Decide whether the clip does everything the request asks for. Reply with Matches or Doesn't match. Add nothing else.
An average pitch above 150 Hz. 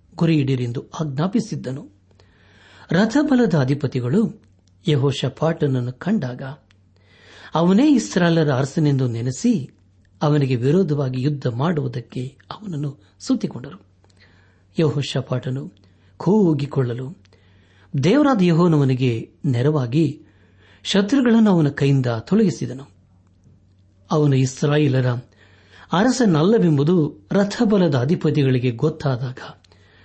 Doesn't match